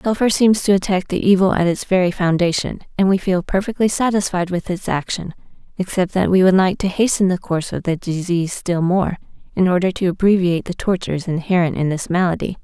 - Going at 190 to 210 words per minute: Yes, average, 200 wpm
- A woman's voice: Yes, female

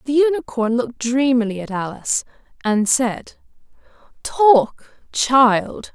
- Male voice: No, female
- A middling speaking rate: No, slow, 100 wpm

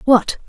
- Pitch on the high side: Yes, high, 240 Hz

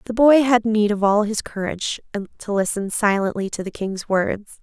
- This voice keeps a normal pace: Yes, average, 195 wpm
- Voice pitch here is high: Yes, high, 210 Hz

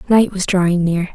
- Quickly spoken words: Yes, fast, 210 wpm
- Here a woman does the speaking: Yes, female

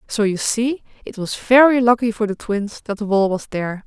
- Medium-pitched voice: No, high, 220 Hz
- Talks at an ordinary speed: No, fast, 235 wpm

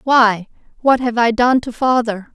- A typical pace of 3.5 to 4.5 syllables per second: Yes, 4.2 syllables/s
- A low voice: No, high, 235 Hz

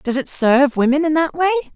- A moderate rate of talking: No, fast, 240 wpm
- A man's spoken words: No, female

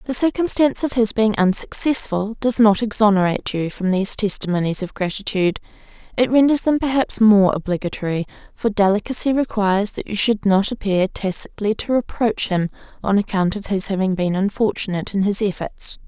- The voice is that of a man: No, female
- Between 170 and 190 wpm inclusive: No, average, 160 wpm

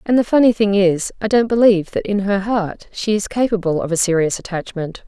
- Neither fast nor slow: No, fast, 225 wpm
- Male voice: No, female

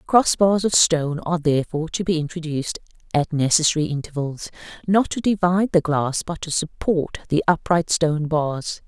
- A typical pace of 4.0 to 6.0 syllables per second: Yes, 5.3 syllables/s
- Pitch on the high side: No, medium, 165 Hz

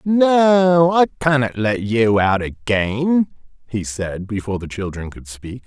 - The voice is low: Yes, low, 130 Hz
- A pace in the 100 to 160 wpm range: Yes, average, 150 wpm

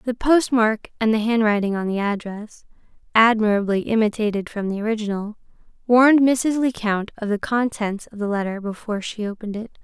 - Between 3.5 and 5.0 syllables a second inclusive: Yes, 4.2 syllables/s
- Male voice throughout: No, female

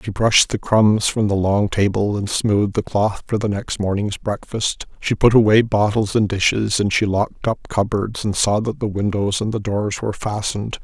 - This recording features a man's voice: Yes, male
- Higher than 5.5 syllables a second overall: No, 5.0 syllables/s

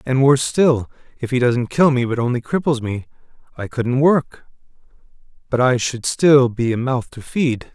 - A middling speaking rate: Yes, average, 185 wpm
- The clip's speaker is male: Yes, male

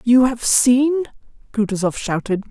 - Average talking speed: No, slow, 120 wpm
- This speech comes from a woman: Yes, female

